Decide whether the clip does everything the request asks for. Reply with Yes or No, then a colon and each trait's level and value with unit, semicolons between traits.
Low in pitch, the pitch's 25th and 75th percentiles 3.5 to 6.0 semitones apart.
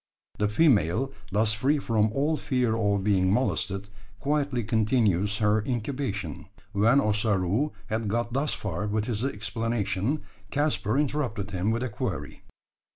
Yes: low, 110 Hz; average, 4.0 semitones